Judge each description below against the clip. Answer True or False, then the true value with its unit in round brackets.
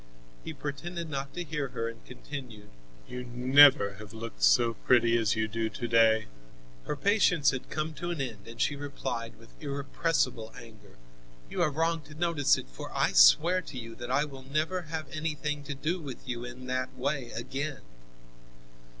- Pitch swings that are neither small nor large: True (4.7 semitones)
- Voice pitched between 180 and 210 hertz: False (135 Hz)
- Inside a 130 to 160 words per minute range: False (180 wpm)